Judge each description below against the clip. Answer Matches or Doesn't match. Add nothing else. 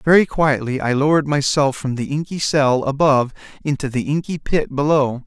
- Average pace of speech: Matches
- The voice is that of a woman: Doesn't match